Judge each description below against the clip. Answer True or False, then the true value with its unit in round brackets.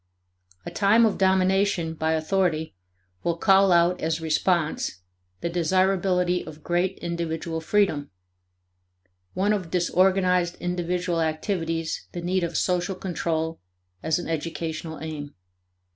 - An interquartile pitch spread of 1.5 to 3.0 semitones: True (2.5 semitones)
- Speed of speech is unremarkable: False (115 wpm)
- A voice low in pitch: False (175 Hz)